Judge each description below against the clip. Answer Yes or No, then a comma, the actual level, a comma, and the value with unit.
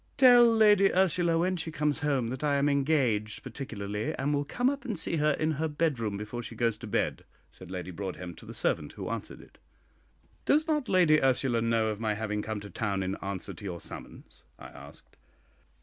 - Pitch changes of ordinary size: No, wide, 7.3 semitones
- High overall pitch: No, low, 135 Hz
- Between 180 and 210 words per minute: Yes, fast, 205 wpm